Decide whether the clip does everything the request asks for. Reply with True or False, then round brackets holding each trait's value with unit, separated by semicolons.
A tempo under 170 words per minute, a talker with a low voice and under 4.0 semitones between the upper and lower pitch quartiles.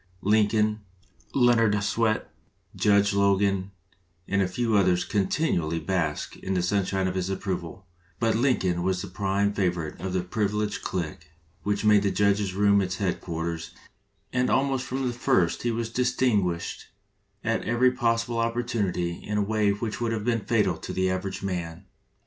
True (160 wpm; 100 Hz; 3.6 semitones)